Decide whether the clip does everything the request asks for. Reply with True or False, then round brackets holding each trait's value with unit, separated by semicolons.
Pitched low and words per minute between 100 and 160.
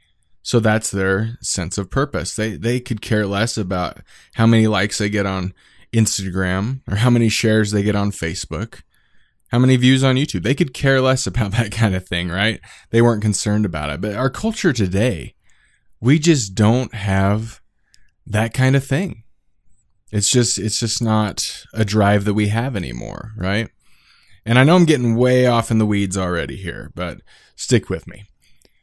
False (110 Hz; 180 wpm)